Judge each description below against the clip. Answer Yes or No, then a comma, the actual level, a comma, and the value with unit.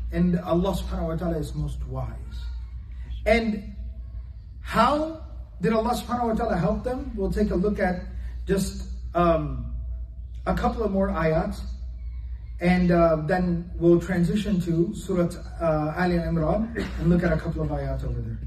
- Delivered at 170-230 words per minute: No, average, 155 wpm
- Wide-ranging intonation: Yes, wide, 6.9 semitones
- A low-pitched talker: No, medium, 170 Hz